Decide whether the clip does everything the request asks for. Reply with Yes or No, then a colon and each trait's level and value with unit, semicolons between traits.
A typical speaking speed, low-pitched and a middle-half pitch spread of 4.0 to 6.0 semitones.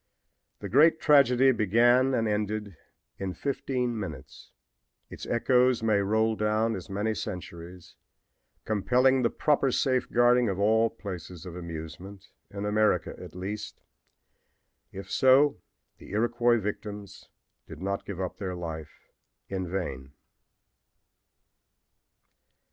No: slow, 115 wpm; low, 105 Hz; average, 4.4 semitones